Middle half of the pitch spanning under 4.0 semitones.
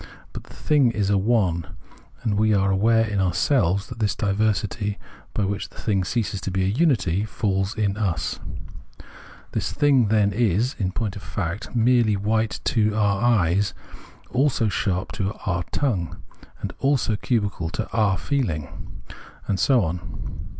Yes: average, 3.0 semitones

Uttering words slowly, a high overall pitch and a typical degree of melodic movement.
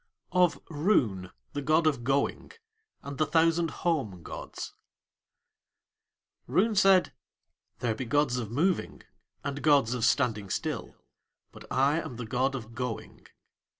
No: slow, 130 wpm; medium, 140 Hz; average, 5.0 semitones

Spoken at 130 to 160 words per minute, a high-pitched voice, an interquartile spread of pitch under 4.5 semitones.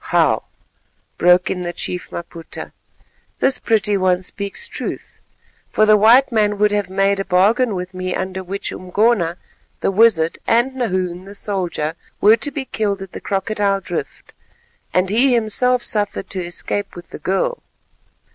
Yes: average, 155 wpm; high, 200 Hz; average, 3.1 semitones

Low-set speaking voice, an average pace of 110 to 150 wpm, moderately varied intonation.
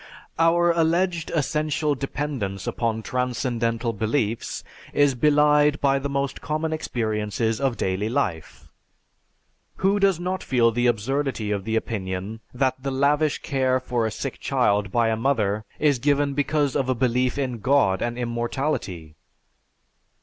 Yes: low, 130 Hz; average, 140 wpm; average, 4.6 semitones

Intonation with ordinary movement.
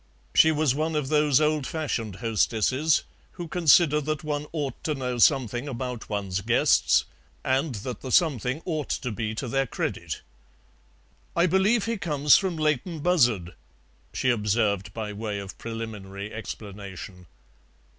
No: wide, 6.0 semitones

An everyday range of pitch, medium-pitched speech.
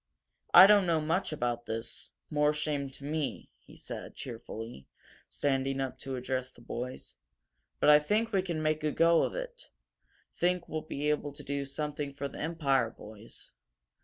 Yes: average, 3.3 semitones; medium, 145 Hz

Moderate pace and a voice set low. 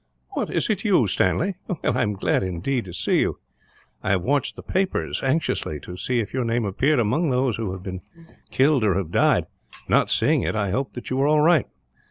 No: fast, 215 wpm; low, 125 Hz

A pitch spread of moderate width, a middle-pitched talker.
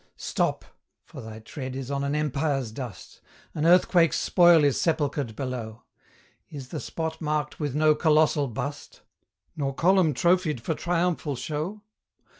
Yes: average, 3.3 semitones; medium, 150 Hz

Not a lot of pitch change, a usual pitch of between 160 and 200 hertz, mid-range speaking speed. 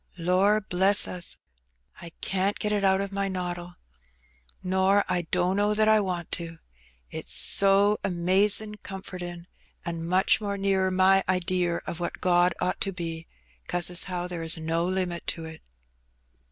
Yes: narrow, 2.0 semitones; medium, 185 Hz; average, 155 wpm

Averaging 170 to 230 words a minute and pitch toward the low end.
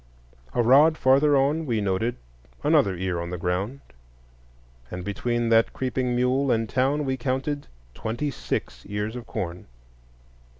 No: average, 140 wpm; low, 120 Hz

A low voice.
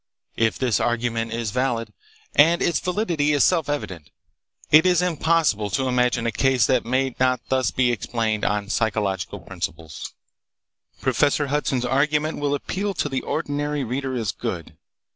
Yes: low, 130 Hz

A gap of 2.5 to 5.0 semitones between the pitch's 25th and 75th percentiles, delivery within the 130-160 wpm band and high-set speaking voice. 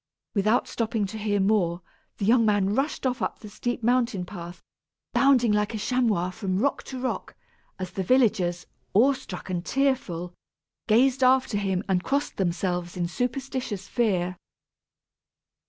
No: wide, 5.4 semitones; average, 150 wpm; high, 210 Hz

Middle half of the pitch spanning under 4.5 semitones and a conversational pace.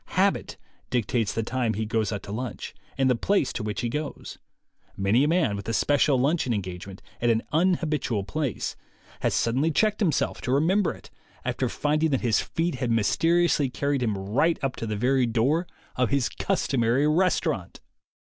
No: average, 5.3 semitones; average, 180 wpm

